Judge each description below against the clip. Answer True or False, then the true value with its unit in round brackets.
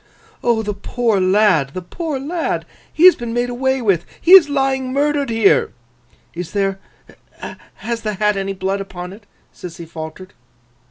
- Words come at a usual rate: True (155 wpm)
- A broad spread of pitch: True (5.7 semitones)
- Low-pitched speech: False (215 Hz)